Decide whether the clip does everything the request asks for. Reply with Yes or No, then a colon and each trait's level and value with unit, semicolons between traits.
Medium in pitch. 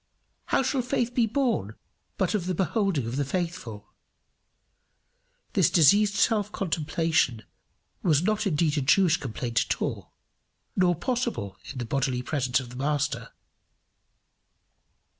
Yes: medium, 165 Hz